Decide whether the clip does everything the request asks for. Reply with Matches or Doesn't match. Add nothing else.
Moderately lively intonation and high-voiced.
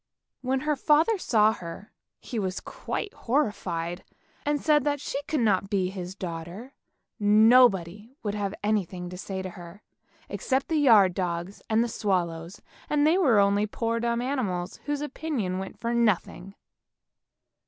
Doesn't match